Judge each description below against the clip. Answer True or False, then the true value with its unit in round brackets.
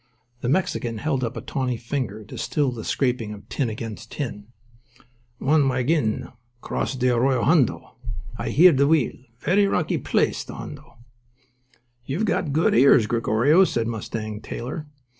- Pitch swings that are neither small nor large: True (4.4 semitones)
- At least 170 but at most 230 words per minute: False (160 wpm)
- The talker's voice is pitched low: True (125 Hz)